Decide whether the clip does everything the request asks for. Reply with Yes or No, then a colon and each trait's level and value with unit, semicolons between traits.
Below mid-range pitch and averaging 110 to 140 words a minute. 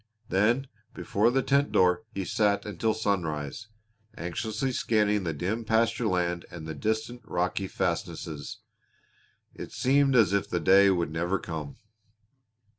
Yes: low, 100 Hz; slow, 135 wpm